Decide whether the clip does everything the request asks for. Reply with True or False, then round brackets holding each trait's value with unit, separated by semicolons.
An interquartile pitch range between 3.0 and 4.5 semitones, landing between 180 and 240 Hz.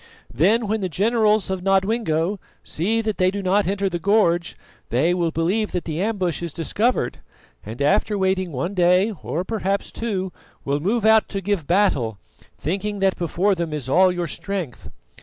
True (3.5 semitones; 190 Hz)